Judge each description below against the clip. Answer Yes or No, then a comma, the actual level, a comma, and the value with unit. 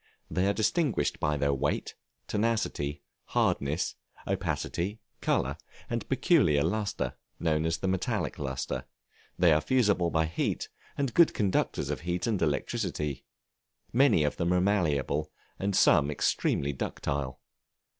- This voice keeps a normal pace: No, slow, 130 wpm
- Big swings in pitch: Yes, wide, 5.7 semitones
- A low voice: Yes, very low, 85 Hz